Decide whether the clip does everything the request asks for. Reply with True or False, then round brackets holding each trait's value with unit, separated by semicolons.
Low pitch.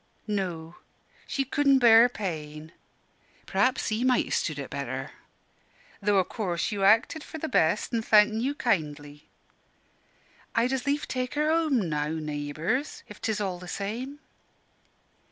False (210 Hz)